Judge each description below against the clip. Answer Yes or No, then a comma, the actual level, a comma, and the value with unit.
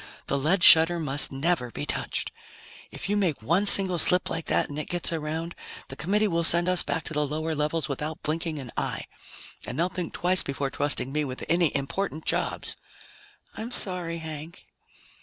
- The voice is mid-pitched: Yes, medium, 160 Hz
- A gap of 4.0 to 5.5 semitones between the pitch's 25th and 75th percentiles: No, average, 3.0 semitones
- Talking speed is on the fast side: No, average, 185 wpm